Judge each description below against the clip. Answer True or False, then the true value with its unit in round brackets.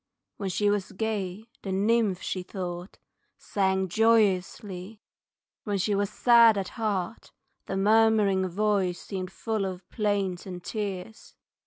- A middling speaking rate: False (130 wpm)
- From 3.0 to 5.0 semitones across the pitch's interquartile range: False (2.5 semitones)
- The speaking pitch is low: False (200 Hz)